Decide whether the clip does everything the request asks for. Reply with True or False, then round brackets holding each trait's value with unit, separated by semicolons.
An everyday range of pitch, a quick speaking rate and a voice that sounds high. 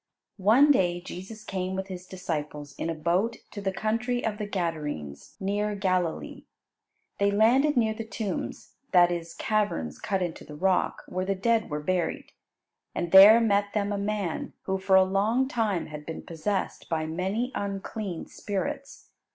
False (3.6 semitones; 165 wpm; 195 Hz)